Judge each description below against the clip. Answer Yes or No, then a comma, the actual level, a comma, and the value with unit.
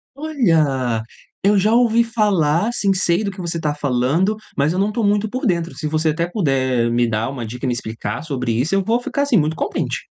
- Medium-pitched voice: Yes, medium, 165 Hz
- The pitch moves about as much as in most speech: No, wide, 8.1 semitones